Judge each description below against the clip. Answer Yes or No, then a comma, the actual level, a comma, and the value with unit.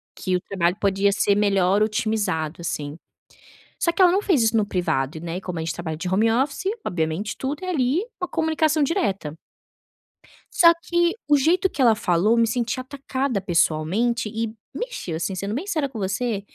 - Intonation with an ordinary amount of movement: No, wide, 7.6 semitones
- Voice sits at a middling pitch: No, high, 215 Hz